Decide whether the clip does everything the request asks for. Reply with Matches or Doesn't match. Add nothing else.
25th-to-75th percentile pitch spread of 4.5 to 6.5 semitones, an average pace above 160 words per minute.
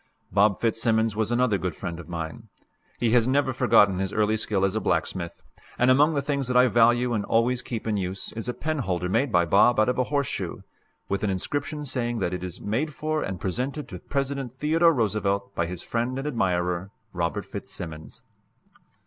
Matches